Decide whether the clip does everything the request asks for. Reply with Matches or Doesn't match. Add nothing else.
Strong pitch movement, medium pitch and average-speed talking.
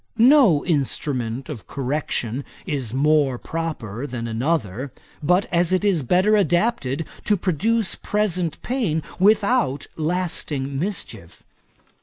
Doesn't match